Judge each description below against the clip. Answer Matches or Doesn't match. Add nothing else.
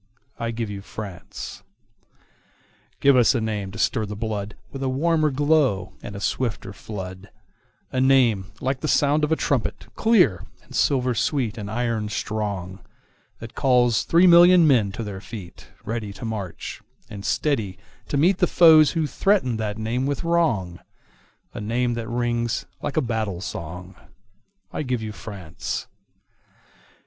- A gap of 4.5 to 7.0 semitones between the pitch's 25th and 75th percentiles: Matches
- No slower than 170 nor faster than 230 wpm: Doesn't match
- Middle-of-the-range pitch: Doesn't match